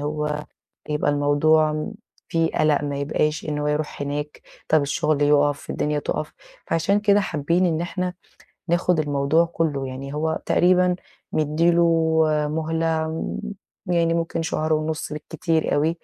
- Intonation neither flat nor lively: No, narrow, 2.1 semitones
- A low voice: No, medium, 155 Hz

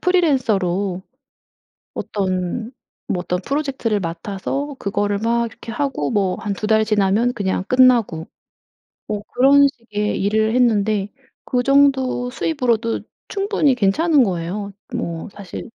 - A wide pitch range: No, average, 4.7 semitones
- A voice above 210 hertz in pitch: Yes, high, 220 Hz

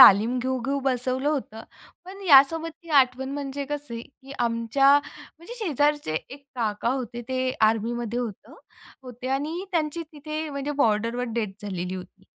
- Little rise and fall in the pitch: No, average, 3.9 semitones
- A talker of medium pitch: No, very high, 260 Hz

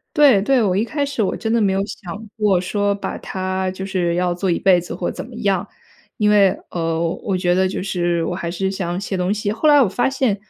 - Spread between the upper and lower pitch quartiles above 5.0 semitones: No, average, 2.9 semitones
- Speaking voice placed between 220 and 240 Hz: No, high, 195 Hz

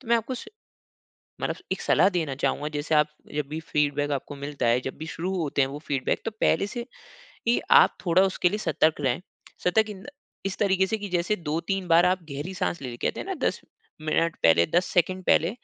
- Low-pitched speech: No, medium, 170 Hz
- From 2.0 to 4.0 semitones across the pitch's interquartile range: No, average, 4.6 semitones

